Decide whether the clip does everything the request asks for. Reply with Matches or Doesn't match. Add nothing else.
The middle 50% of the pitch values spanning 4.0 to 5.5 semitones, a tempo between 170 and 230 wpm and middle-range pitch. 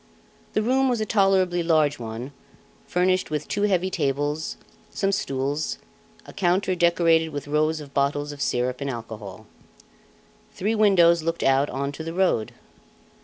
Doesn't match